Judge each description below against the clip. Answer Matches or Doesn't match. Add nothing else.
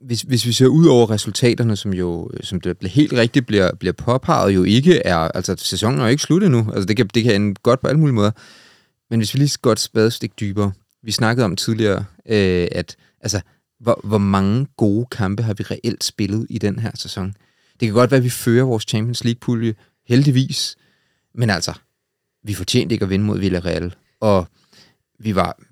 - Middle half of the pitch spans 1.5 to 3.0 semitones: Doesn't match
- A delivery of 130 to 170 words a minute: Doesn't match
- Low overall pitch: Matches